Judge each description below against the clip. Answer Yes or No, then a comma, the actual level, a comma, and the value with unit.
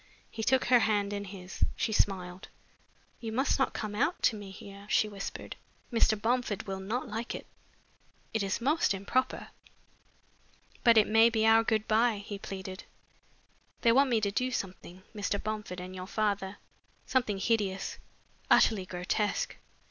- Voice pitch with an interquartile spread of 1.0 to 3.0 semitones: Yes, average, 2.7 semitones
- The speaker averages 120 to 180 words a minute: Yes, average, 155 wpm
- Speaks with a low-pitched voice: No, high, 210 Hz